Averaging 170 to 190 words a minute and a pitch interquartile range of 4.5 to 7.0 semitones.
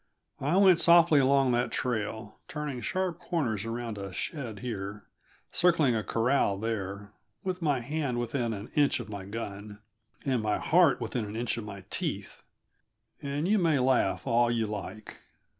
No: average, 160 wpm; average, 5.3 semitones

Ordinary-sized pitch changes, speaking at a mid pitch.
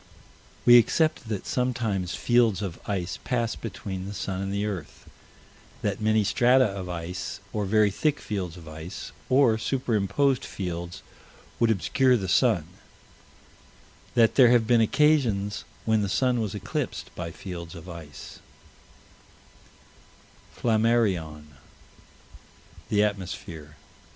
No: average, 4.6 semitones; low, 105 Hz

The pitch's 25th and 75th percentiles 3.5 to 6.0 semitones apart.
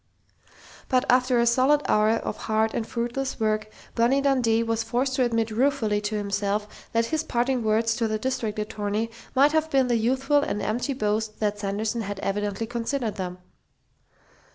No: average, 3.1 semitones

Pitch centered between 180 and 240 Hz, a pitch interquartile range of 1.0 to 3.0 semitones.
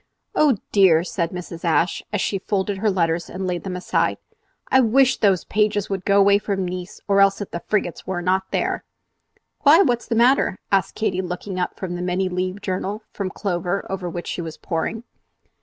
Yes: high, 190 Hz; narrow, 2.4 semitones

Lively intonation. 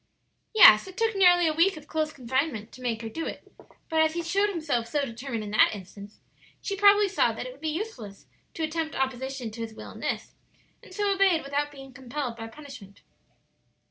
Yes: wide, 6.2 semitones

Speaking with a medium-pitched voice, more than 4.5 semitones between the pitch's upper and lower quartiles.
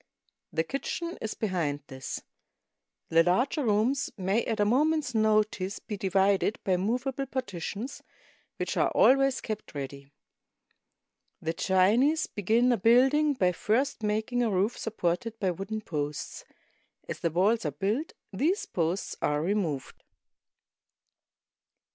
No: high, 210 Hz; wide, 5.4 semitones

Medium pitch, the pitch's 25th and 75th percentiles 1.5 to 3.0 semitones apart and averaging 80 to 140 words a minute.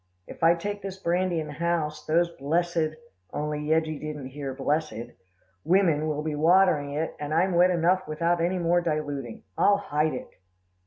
No: medium, 160 Hz; narrow, 2.6 semitones; average, 170 wpm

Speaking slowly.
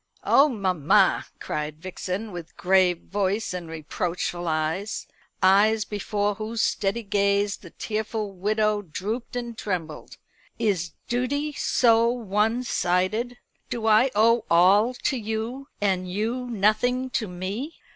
Yes: slow, 125 wpm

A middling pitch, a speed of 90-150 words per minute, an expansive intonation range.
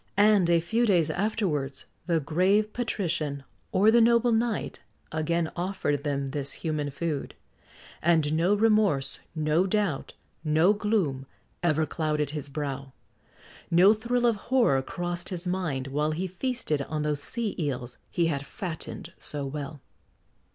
Yes: medium, 165 Hz; average, 140 wpm; wide, 5.8 semitones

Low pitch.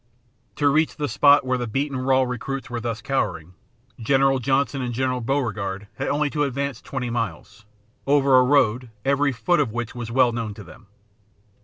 Yes: low, 130 Hz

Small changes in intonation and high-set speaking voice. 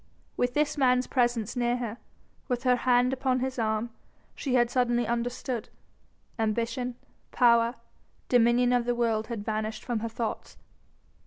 Yes: narrow, 1.4 semitones; high, 240 Hz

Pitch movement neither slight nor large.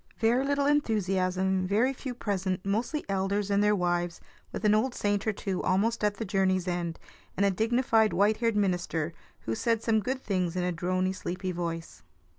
Yes: average, 3.4 semitones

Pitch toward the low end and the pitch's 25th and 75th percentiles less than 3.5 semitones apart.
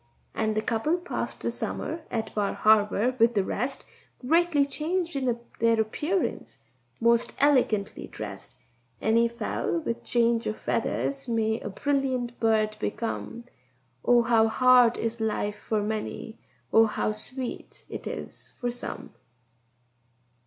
No: high, 235 Hz; average, 2.9 semitones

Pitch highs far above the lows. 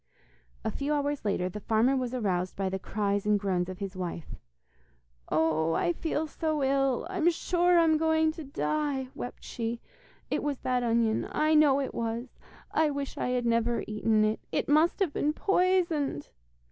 Yes: wide, 6.4 semitones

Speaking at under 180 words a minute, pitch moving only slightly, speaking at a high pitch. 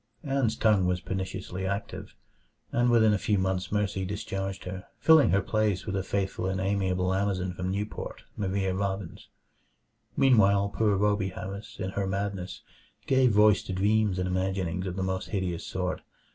No: average, 160 wpm; narrow, 1.7 semitones; very low, 95 Hz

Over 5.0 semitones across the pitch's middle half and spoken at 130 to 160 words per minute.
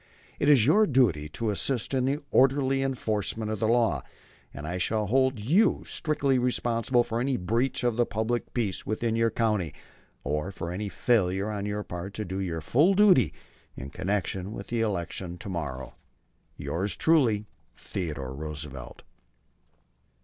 Yes: wide, 5.6 semitones; average, 155 wpm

